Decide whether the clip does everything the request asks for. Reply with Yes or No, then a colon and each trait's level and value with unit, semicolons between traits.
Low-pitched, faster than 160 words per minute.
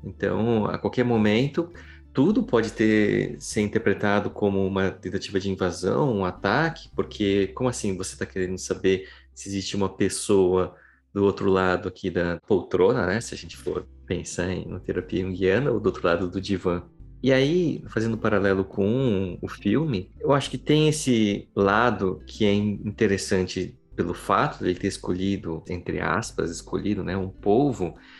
Yes: very low, 95 Hz; average, 170 wpm